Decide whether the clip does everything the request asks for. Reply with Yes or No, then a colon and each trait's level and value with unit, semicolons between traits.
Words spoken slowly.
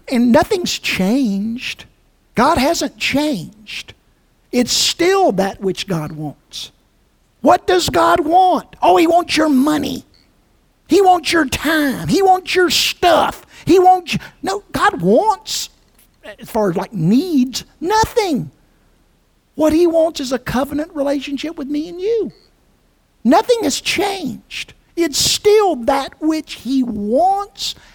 Yes: slow, 130 wpm